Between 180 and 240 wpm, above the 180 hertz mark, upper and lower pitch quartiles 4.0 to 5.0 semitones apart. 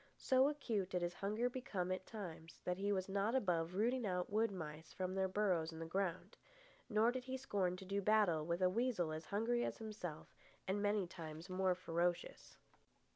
No: average, 190 wpm; high, 190 Hz; average, 3.5 semitones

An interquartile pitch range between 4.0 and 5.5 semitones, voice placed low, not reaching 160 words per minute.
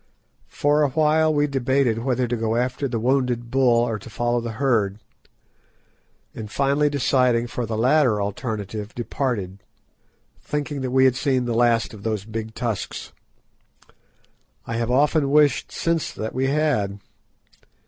No: average, 3.6 semitones; low, 125 Hz; average, 145 wpm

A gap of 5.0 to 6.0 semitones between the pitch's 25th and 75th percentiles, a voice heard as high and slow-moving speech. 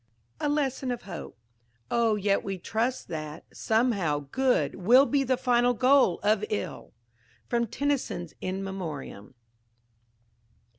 Yes: wide, 5.4 semitones; high, 225 Hz; slow, 120 wpm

